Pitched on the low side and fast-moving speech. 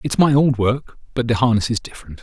Yes: low, 120 Hz; fast, 240 wpm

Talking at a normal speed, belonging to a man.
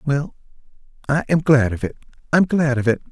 Yes: average, 175 wpm; male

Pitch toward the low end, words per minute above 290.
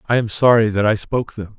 No: low, 110 Hz; fast, 265 wpm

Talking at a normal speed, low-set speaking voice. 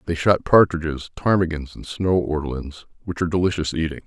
Yes: average, 165 wpm; very low, 85 Hz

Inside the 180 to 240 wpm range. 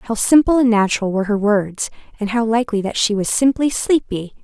Yes: fast, 205 wpm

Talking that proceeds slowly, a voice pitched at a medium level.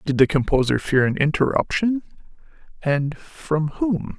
Yes: slow, 115 wpm; medium, 160 Hz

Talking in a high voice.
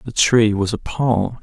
No: low, 110 Hz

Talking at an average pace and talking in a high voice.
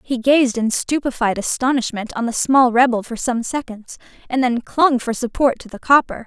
Yes: average, 190 wpm; high, 245 Hz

